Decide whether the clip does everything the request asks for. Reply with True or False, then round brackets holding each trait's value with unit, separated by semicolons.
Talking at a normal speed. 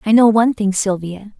False (215 wpm)